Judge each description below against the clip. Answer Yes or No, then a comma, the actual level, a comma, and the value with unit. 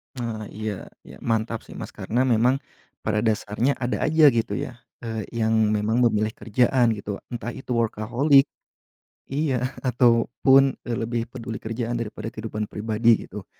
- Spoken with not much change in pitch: Yes, narrow, 2.2 semitones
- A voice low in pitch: Yes, low, 115 Hz